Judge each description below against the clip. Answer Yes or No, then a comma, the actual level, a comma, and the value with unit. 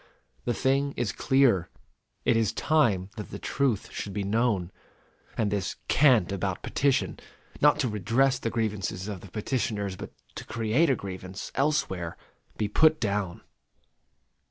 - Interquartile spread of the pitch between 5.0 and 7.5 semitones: Yes, average, 5.3 semitones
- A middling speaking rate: Yes, average, 145 wpm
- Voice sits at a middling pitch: No, low, 110 Hz